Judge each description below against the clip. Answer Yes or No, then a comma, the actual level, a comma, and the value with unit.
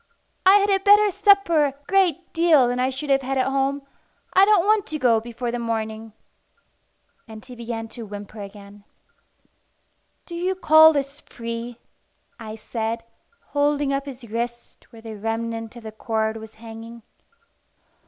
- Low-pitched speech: No, high, 245 Hz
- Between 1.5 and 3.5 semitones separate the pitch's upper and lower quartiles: No, average, 5.2 semitones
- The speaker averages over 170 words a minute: No, average, 160 wpm